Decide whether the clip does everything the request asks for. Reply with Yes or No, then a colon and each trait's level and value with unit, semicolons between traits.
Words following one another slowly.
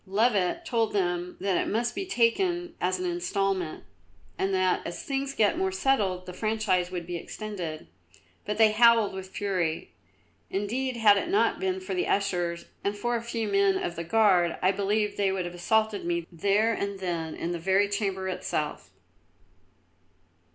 No: average, 170 wpm